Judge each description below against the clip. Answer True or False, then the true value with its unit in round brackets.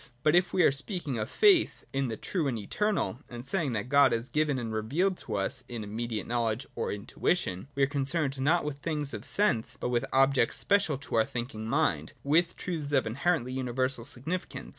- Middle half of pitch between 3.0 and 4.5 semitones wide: False (5.1 semitones)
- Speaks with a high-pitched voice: False (135 Hz)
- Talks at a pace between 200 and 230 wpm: True (205 wpm)